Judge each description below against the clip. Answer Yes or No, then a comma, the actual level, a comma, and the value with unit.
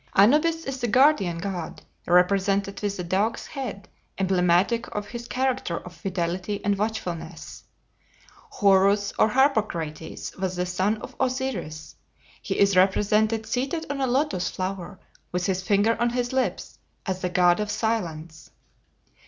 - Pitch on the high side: Yes, high, 200 Hz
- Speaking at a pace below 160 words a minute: Yes, average, 140 wpm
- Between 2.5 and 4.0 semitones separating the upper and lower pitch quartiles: No, average, 4.8 semitones